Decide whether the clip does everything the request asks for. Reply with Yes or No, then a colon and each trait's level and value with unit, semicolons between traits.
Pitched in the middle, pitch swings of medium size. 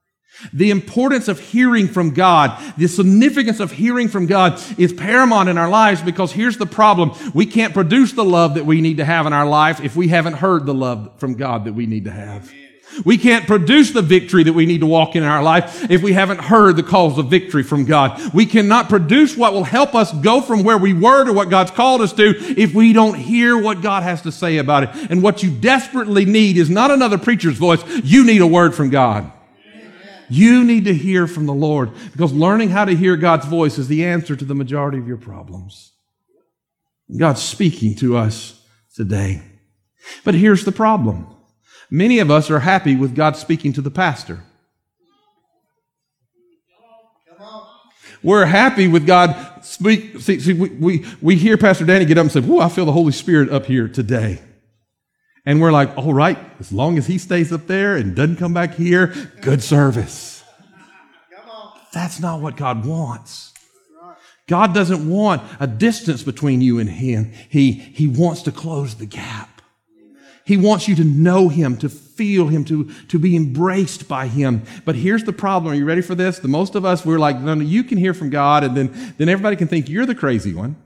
No: medium, 170 Hz; wide, 6.1 semitones